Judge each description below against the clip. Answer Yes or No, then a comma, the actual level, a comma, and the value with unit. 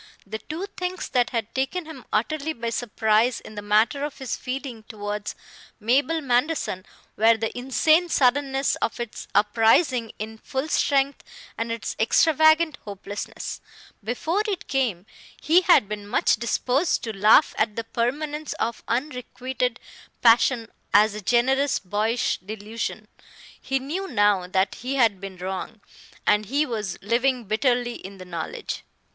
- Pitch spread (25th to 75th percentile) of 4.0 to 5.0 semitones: Yes, average, 4.5 semitones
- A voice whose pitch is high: Yes, high, 240 Hz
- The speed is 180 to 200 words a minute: No, average, 145 wpm